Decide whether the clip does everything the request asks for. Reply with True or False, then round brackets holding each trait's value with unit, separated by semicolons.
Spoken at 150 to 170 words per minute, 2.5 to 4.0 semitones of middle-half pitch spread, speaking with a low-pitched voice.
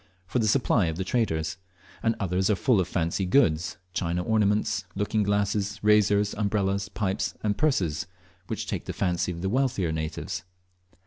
True (165 wpm; 3.0 semitones; 100 Hz)